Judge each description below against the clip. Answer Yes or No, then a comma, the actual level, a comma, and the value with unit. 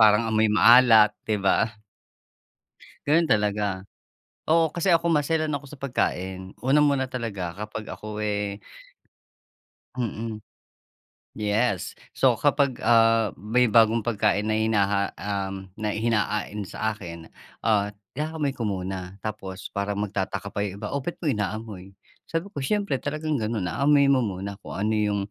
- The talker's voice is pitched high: No, low, 110 Hz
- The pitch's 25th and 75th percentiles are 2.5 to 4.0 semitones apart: No, average, 4.7 semitones